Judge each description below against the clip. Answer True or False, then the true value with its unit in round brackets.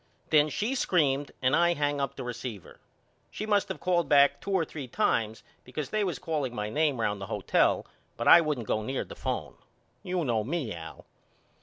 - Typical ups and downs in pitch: False (6.3 semitones)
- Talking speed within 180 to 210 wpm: True (190 wpm)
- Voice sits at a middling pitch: True (145 Hz)